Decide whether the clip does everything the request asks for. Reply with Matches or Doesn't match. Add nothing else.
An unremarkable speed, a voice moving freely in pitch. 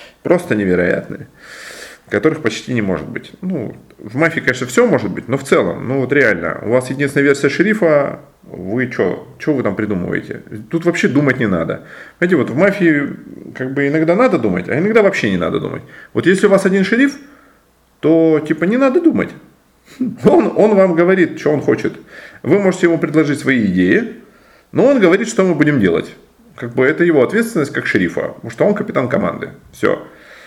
Doesn't match